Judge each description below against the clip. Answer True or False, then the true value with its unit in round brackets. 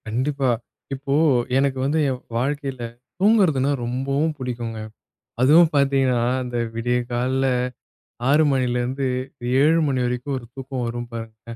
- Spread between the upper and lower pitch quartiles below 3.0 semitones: True (2.4 semitones)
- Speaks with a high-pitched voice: False (130 Hz)